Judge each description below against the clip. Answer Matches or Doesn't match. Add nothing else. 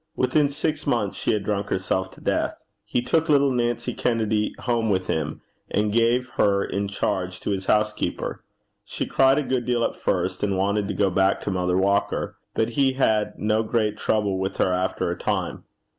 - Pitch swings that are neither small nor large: Matches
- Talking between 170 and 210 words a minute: Matches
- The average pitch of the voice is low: Matches